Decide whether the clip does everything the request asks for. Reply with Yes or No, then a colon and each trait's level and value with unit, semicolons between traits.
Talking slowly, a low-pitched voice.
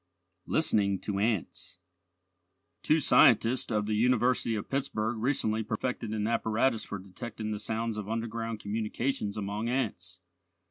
Yes: slow, 130 wpm; low, 110 Hz